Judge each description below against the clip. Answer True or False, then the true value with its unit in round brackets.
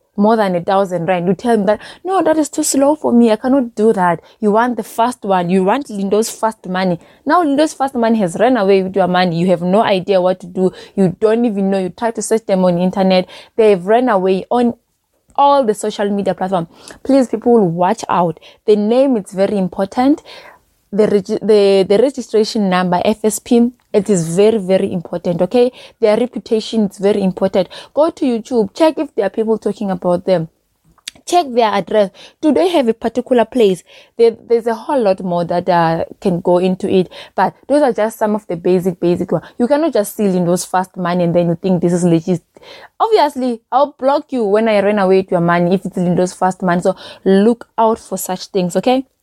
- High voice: True (210 Hz)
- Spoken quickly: True (215 wpm)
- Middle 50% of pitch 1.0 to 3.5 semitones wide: False (4.2 semitones)